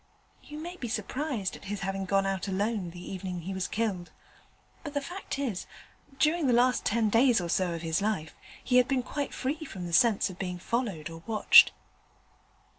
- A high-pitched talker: Yes, high, 210 Hz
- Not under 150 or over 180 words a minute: No, average, 200 wpm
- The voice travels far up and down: Yes, wide, 5.8 semitones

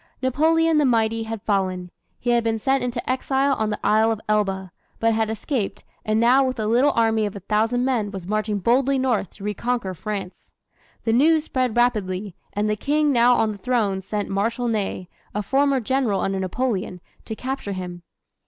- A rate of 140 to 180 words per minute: No, average, 190 wpm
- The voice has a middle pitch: No, high, 225 Hz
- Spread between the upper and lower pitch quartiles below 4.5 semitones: Yes, average, 3.9 semitones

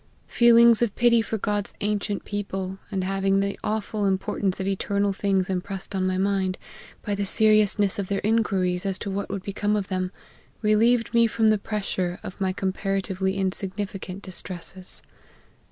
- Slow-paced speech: No, average, 160 wpm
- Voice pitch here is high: Yes, high, 195 Hz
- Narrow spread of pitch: Yes, narrow, 1.8 semitones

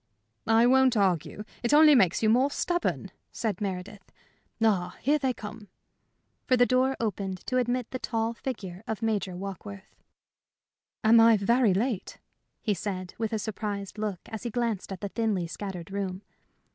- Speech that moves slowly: No, average, 160 wpm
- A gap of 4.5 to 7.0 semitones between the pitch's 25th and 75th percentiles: No, average, 3.8 semitones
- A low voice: No, high, 215 Hz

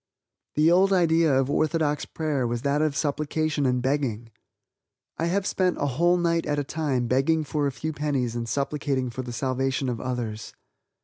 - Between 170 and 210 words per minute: Yes, average, 180 wpm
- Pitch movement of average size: Yes, average, 3.6 semitones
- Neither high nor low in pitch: Yes, medium, 145 Hz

